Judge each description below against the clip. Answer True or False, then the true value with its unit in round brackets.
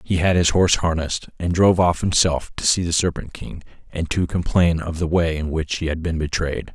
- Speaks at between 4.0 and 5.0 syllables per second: False (5.4 syllables/s)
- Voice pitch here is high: False (85 Hz)